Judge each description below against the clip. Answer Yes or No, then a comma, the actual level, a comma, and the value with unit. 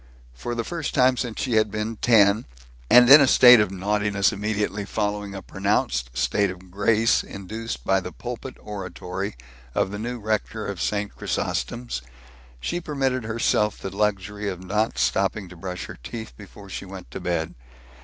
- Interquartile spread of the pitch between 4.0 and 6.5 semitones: No, average, 2.8 semitones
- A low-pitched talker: Yes, low, 105 Hz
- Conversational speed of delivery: Yes, average, 170 wpm